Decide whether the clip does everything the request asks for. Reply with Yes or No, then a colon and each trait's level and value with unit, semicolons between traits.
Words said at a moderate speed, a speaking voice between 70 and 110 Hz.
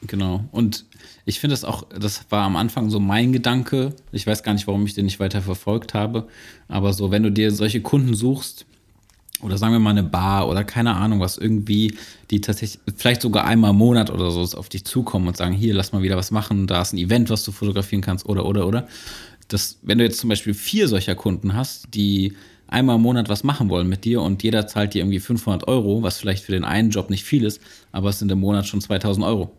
No: fast, 235 wpm; low, 105 Hz